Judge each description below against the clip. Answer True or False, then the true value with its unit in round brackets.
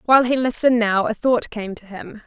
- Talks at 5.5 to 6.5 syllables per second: True (5.7 syllables/s)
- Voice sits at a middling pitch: False (230 Hz)